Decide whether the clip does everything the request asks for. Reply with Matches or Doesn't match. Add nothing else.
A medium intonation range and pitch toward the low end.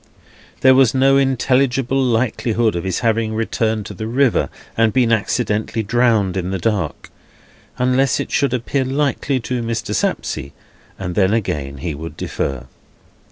Matches